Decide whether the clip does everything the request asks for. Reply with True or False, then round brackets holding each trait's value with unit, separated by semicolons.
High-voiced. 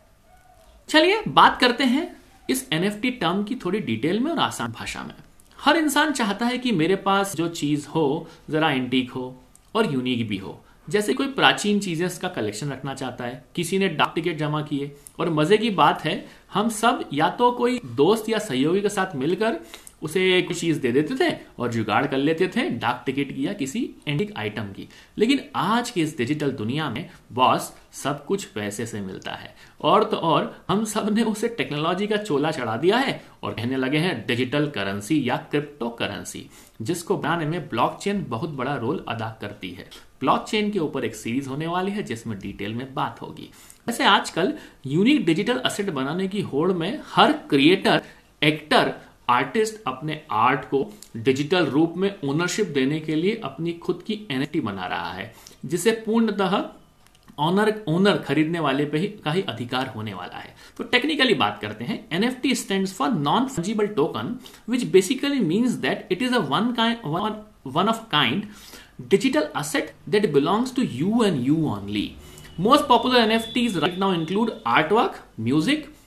False (175 Hz)